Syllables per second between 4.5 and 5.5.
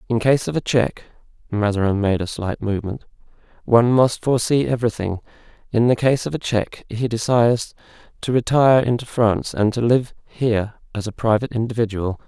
Yes: 5.1 syllables/s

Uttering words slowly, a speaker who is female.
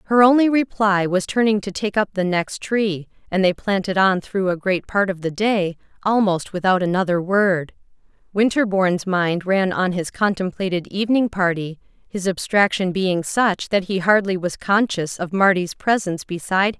No: average, 170 wpm; female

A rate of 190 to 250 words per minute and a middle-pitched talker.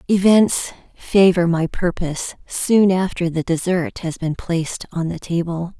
No: average, 145 wpm; medium, 175 Hz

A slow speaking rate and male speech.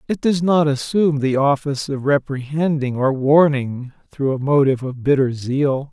No: average, 160 wpm; male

